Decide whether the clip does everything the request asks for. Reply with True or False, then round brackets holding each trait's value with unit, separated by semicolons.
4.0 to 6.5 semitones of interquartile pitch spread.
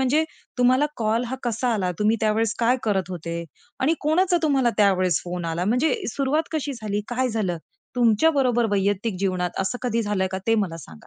True (5.1 semitones)